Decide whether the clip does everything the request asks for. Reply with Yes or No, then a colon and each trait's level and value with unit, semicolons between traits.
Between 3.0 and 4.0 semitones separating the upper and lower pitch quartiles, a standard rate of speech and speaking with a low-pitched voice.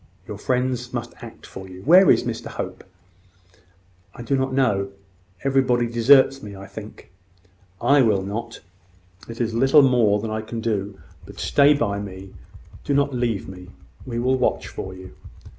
No: average, 4.5 semitones; average, 160 wpm; low, 115 Hz